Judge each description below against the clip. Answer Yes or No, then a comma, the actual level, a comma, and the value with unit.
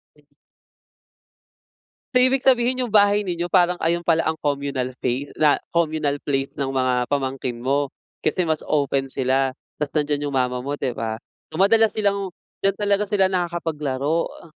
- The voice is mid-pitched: Yes, medium, 150 Hz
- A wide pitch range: Yes, wide, 5.8 semitones